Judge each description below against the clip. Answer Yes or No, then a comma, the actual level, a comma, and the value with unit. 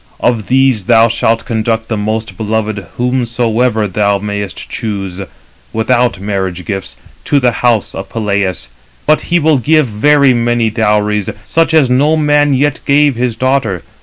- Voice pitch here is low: Yes, low, 115 Hz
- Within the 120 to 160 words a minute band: Yes, average, 150 wpm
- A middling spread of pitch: Yes, average, 3.8 semitones